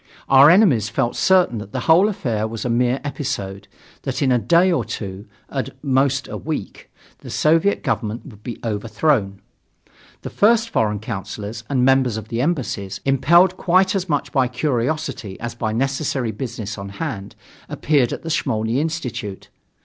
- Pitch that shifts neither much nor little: No, wide, 5.9 semitones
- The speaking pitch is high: No, low, 125 Hz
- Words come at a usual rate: Yes, average, 165 wpm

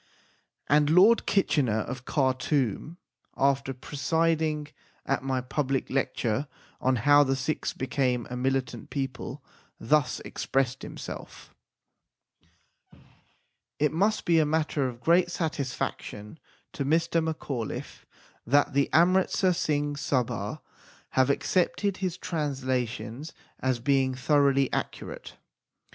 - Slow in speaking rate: Yes, slow, 110 wpm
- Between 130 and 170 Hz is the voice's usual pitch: Yes, medium, 140 Hz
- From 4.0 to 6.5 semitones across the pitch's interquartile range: No, average, 3.5 semitones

